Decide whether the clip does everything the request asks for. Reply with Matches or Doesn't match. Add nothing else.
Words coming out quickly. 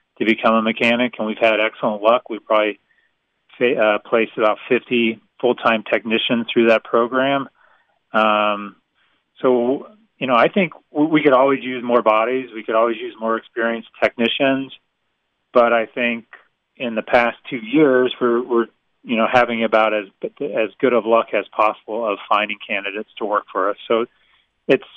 Doesn't match